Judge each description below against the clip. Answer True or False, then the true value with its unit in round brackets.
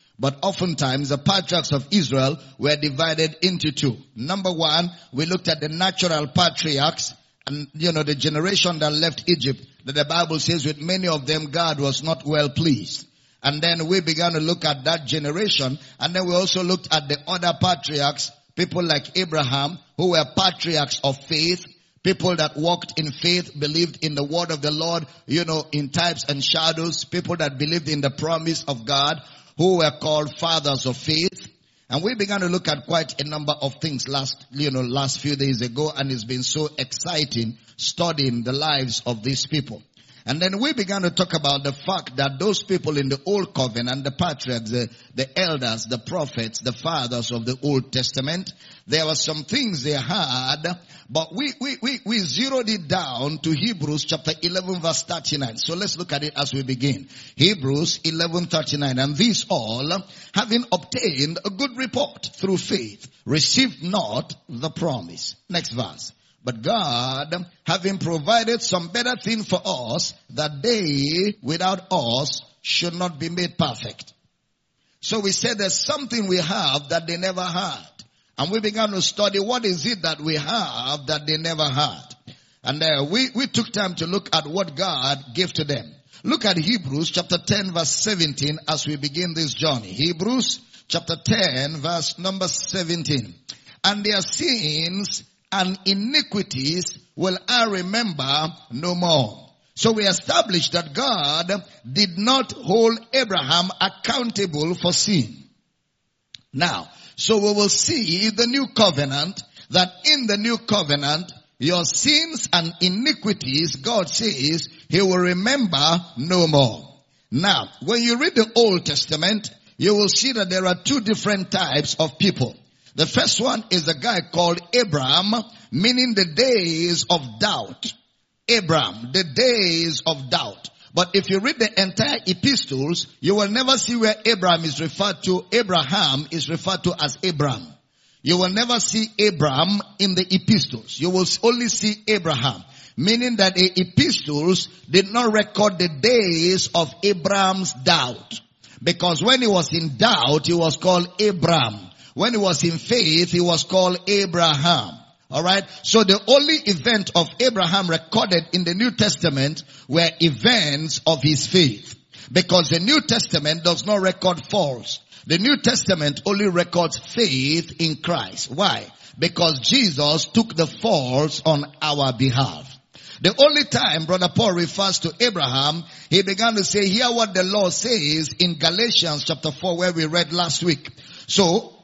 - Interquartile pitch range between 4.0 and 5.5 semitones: True (4.7 semitones)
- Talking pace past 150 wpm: True (165 wpm)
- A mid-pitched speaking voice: True (170 Hz)